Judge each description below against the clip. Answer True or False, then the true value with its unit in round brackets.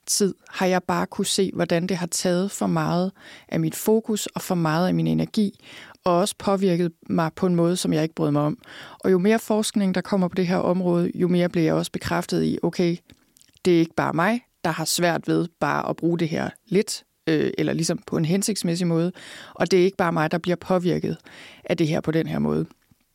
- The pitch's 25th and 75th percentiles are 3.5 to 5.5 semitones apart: False (2.4 semitones)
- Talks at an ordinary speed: False (235 wpm)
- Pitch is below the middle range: False (175 Hz)